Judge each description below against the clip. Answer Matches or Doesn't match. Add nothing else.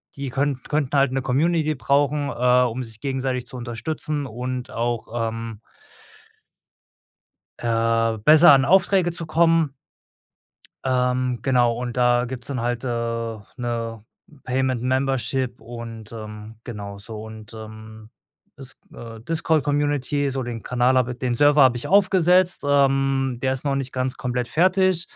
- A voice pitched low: Matches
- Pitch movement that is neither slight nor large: Matches